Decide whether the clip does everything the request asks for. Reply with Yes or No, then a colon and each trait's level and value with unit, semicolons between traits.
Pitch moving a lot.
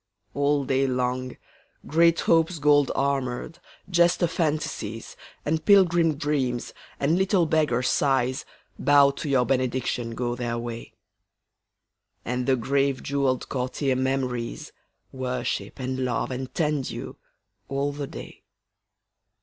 No: average, 2.9 semitones